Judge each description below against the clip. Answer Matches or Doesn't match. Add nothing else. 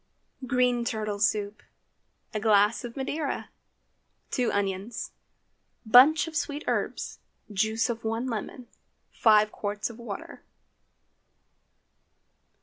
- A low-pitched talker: Doesn't match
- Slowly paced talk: Matches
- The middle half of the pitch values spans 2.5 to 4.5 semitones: Matches